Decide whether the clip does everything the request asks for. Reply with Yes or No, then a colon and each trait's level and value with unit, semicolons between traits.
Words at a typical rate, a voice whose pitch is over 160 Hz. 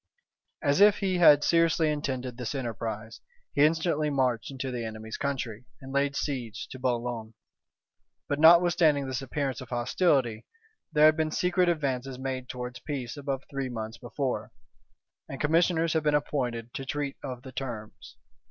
No: average, 155 wpm; low, 135 Hz